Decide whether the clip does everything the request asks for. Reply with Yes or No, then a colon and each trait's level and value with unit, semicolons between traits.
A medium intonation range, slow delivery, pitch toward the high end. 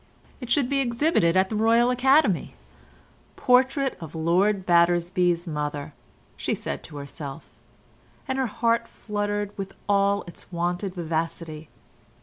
No: wide, 5.8 semitones; slow, 130 wpm; high, 195 Hz